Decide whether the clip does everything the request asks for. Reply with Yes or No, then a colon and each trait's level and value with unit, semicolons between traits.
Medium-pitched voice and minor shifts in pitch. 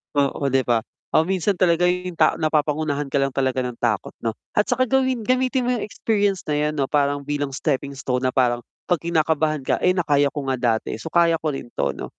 No: medium, 150 Hz; average, 4.8 semitones